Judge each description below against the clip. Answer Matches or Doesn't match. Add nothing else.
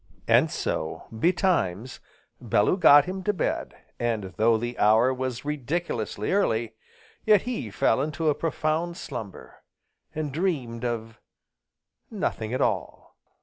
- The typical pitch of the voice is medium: Doesn't match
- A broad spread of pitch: Matches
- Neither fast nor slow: Doesn't match